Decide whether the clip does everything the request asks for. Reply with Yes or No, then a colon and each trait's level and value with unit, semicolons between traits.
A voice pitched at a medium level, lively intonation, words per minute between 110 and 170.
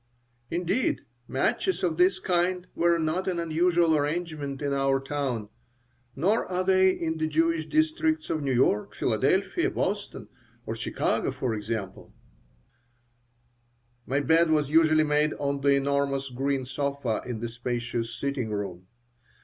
No: medium, 145 Hz; average, 4.3 semitones; slow, 135 wpm